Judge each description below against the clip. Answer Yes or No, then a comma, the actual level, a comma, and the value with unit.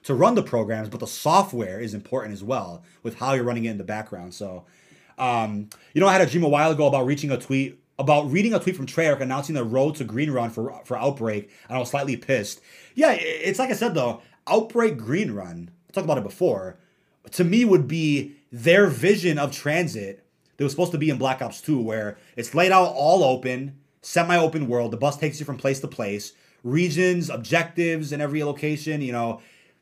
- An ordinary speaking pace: No, fast, 215 wpm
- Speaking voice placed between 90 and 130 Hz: No, medium, 140 Hz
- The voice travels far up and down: Yes, wide, 5.9 semitones